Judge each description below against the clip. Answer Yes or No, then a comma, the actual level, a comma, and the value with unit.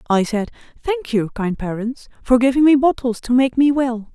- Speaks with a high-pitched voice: Yes, very high, 250 Hz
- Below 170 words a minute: No, fast, 205 wpm